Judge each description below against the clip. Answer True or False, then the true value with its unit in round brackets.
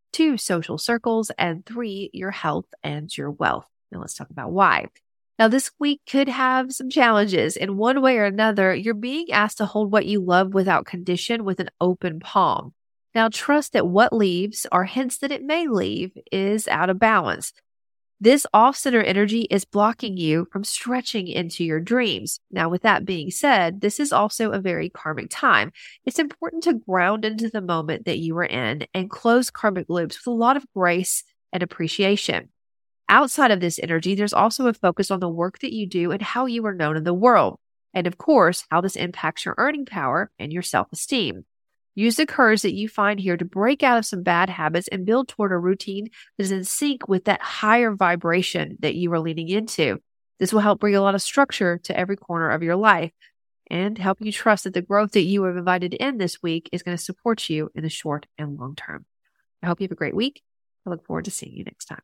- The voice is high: True (200 Hz)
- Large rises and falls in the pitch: False (4.5 semitones)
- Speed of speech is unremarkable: False (215 wpm)